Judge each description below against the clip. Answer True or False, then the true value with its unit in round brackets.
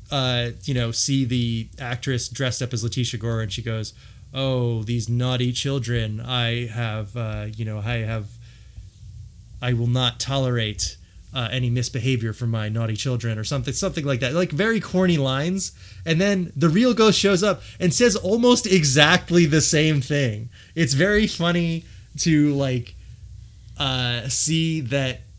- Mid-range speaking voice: False (125 Hz)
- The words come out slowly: False (160 wpm)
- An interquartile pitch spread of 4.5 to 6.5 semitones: True (5.2 semitones)